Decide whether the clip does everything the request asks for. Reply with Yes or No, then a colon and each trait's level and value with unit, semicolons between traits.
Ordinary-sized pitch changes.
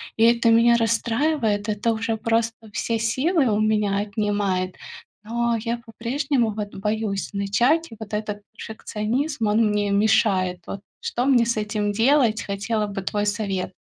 No: narrow, 2.1 semitones